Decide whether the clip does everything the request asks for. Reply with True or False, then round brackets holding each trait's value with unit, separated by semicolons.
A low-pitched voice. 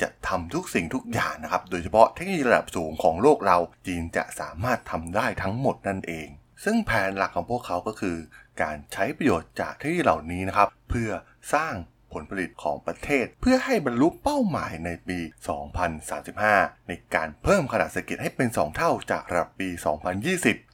True (95 Hz)